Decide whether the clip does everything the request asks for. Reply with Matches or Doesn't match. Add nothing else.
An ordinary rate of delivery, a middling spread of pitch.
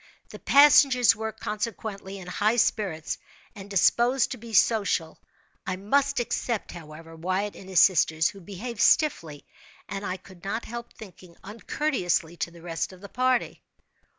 Matches